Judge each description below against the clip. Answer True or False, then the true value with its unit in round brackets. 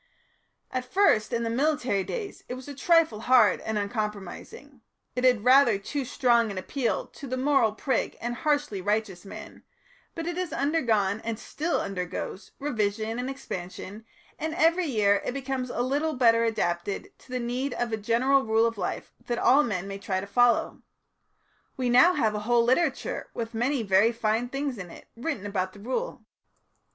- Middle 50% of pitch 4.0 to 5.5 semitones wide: True (4.5 semitones)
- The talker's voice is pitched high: True (240 Hz)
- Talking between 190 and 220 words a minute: False (180 wpm)